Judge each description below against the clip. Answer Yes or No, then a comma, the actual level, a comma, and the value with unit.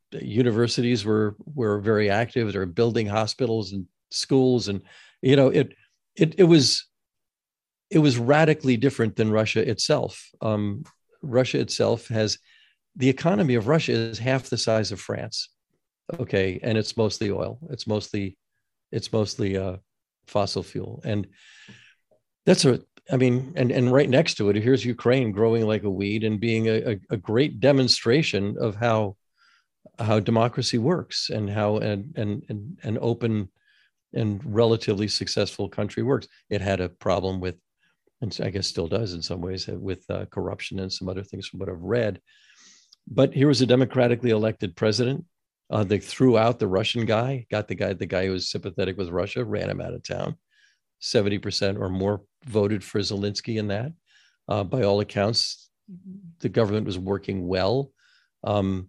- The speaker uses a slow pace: No, average, 165 wpm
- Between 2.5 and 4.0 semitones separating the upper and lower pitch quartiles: Yes, average, 3.7 semitones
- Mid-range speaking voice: No, low, 110 Hz